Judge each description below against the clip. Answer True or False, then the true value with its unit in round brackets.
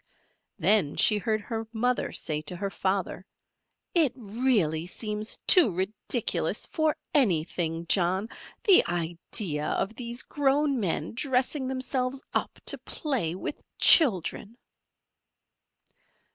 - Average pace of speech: False (115 wpm)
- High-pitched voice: True (215 Hz)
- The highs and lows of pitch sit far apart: True (6.6 semitones)